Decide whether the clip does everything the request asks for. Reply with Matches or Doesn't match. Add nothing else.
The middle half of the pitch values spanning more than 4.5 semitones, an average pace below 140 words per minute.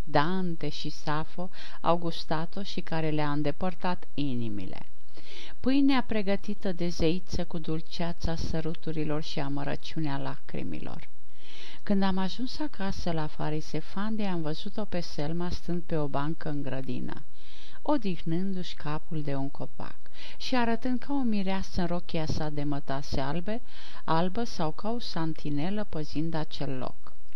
Doesn't match